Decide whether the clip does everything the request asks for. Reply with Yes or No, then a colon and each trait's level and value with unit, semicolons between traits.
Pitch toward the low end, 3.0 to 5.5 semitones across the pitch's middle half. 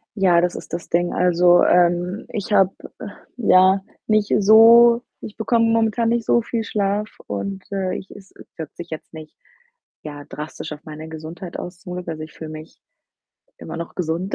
No: medium, 180 Hz; average, 4.2 semitones